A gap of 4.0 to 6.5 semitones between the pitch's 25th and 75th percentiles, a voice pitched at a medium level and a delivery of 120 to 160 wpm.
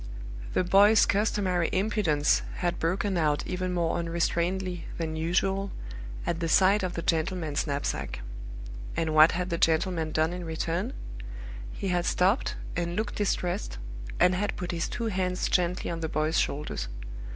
No: narrow, 2.5 semitones; medium, 175 Hz; average, 150 wpm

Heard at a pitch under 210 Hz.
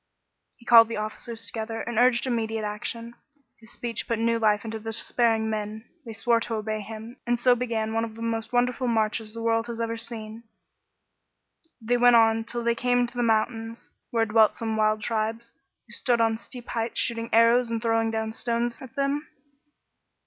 No: high, 230 Hz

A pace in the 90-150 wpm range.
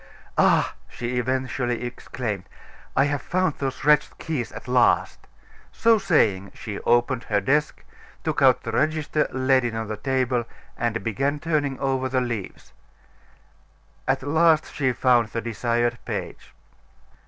Yes: average, 140 wpm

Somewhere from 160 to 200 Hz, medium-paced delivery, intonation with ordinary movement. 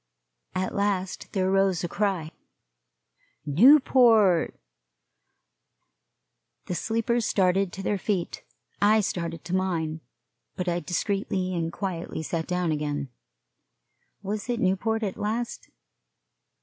No: high, 190 Hz; slow, 110 wpm; average, 3.3 semitones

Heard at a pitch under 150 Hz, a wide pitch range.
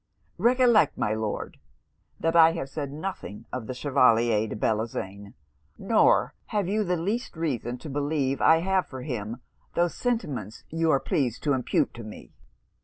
Yes: medium, 140 Hz; wide, 6.6 semitones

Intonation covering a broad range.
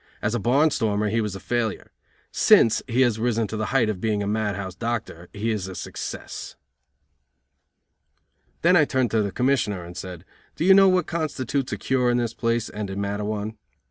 No: average, 3.5 semitones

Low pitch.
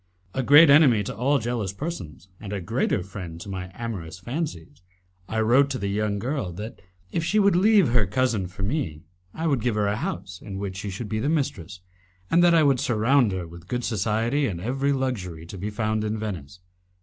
Yes: low, 110 Hz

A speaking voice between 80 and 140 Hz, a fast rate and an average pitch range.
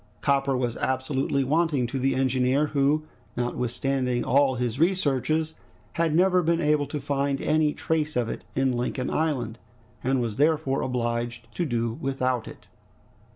No: low, 135 Hz; average, 150 wpm; average, 3.3 semitones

